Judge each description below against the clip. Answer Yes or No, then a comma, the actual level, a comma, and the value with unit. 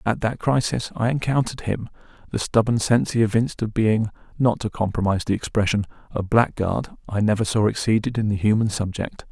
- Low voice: Yes, low, 110 Hz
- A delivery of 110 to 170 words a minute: Yes, average, 165 wpm